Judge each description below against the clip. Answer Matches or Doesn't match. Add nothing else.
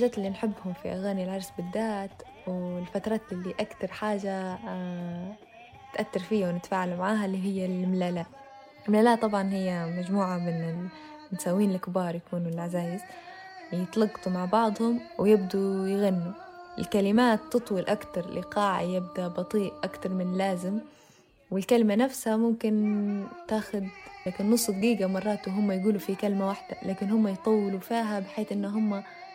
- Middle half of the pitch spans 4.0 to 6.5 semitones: Doesn't match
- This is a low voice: Doesn't match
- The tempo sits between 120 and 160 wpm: Matches